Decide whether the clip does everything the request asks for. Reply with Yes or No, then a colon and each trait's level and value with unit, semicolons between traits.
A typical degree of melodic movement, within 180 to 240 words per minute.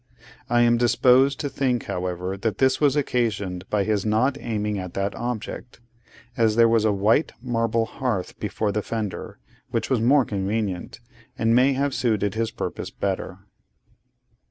No: average, 3.4 semitones; average, 155 wpm